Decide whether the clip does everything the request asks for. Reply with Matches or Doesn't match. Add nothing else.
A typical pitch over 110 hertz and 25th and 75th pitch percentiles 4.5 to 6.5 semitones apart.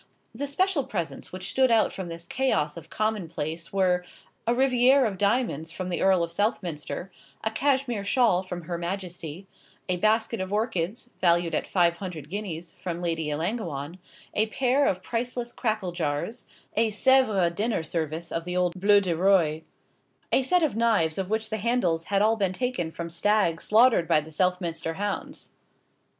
Matches